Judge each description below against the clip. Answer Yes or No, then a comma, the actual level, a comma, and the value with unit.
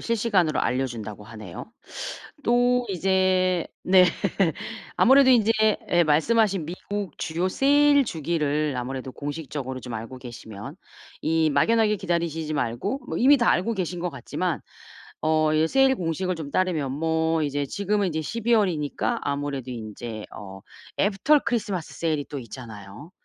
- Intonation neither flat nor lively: No, wide, 6.5 semitones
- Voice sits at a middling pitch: Yes, medium, 160 Hz